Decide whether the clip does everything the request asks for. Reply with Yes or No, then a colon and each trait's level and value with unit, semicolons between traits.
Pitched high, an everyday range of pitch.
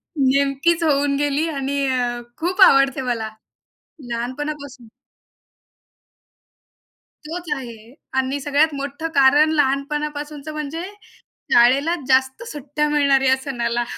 No: very high, 280 Hz; narrow, 2.2 semitones